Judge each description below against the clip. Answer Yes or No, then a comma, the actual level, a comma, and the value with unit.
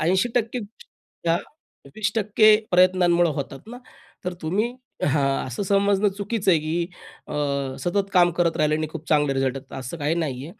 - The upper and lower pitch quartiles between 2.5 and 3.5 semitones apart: No, average, 4.8 semitones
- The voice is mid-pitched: Yes, medium, 175 Hz